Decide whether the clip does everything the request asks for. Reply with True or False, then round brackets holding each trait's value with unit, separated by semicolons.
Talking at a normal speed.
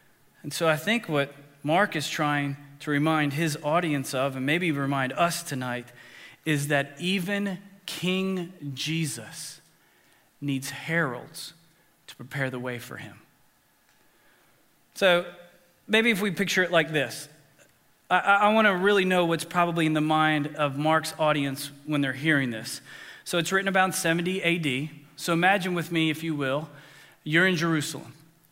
True (155 wpm)